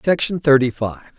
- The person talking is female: No, male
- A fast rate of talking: No, average, 150 wpm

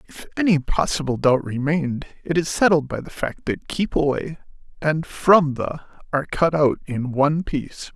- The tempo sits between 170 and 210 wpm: Yes, average, 175 wpm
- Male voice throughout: Yes, male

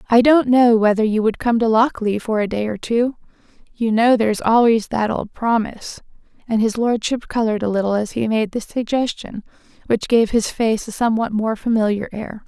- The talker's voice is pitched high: Yes, high, 225 Hz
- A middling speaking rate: Yes, average, 195 wpm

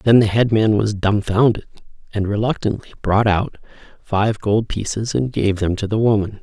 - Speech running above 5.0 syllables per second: No, 4.9 syllables/s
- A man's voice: Yes, male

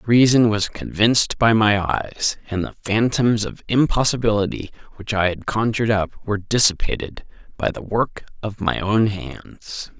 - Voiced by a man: Yes, male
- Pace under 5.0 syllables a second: Yes, 4.6 syllables/s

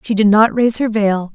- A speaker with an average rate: No, fast, 265 wpm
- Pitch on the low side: No, high, 215 Hz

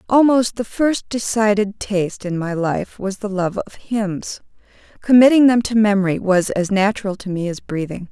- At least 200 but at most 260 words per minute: No, average, 180 wpm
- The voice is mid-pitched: No, high, 205 Hz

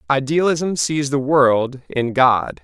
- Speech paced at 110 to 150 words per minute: Yes, slow, 135 wpm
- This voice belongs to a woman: No, male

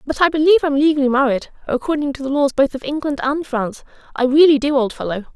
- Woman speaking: Yes, female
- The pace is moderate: No, fast, 225 wpm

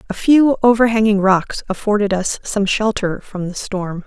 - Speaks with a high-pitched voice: Yes, high, 205 Hz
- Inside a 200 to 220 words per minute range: No, average, 160 wpm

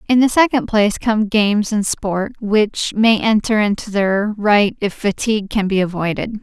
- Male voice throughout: No, female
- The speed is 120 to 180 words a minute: Yes, average, 175 wpm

